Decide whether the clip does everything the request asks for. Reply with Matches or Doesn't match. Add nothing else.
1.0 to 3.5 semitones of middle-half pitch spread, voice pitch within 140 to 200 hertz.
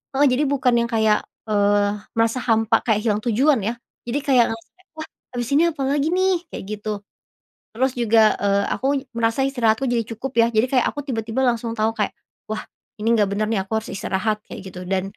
Doesn't match